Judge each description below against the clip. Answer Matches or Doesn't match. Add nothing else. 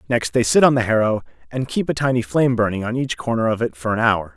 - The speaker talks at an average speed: Doesn't match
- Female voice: Doesn't match